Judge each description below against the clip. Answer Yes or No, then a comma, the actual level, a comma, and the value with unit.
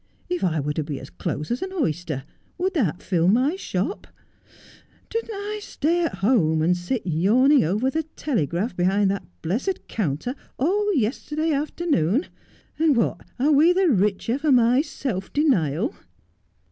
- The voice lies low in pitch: No, high, 245 Hz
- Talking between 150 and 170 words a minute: Yes, average, 160 wpm